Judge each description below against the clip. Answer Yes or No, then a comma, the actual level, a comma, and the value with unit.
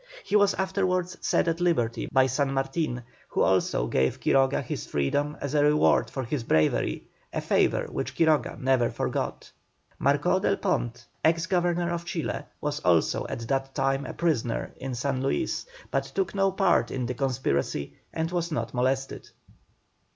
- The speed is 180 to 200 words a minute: No, average, 165 wpm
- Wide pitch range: No, average, 5.0 semitones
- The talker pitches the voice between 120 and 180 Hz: Yes, medium, 140 Hz